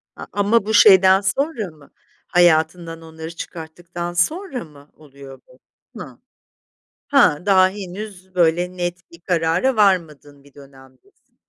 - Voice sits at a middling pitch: Yes, medium, 175 Hz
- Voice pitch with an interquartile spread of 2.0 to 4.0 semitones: Yes, average, 3.5 semitones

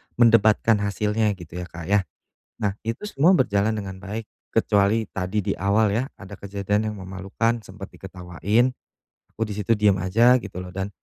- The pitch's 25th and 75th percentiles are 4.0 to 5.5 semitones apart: No, narrow, 2.5 semitones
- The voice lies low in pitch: Yes, low, 105 Hz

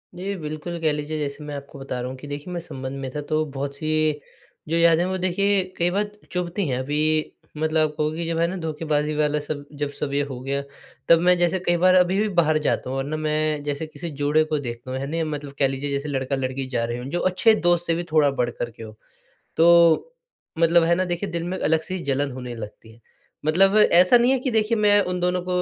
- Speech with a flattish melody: No, average, 3.7 semitones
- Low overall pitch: No, medium, 155 Hz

